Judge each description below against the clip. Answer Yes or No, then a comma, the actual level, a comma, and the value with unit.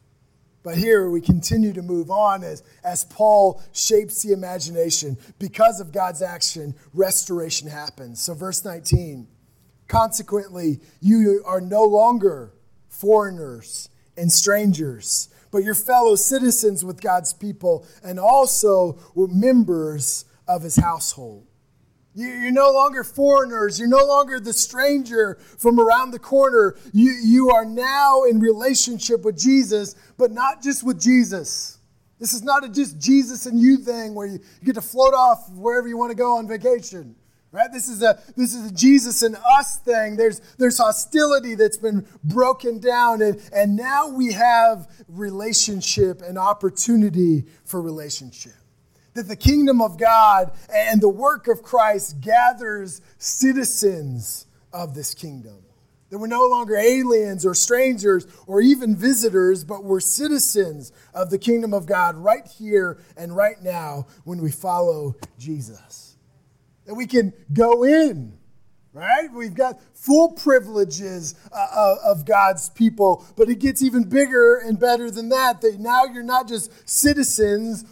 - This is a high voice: Yes, high, 210 Hz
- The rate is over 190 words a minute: No, average, 145 wpm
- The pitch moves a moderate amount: No, wide, 5.9 semitones